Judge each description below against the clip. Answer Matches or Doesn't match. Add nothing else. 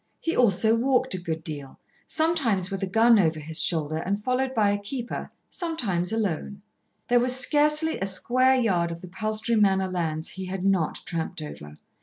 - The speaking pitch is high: Matches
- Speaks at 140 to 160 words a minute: Doesn't match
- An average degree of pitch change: Doesn't match